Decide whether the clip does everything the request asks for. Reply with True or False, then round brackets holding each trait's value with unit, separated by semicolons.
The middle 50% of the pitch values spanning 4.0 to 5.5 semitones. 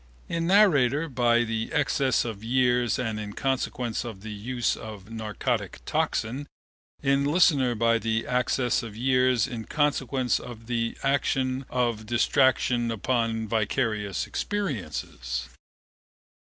False (2.8 semitones)